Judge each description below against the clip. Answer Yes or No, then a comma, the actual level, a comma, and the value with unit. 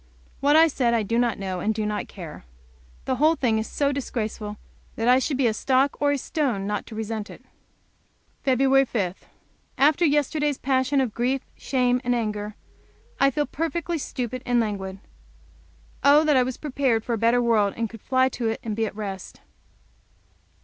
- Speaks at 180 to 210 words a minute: Yes, average, 185 wpm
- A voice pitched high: Yes, high, 245 Hz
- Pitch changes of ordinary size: Yes, average, 4.0 semitones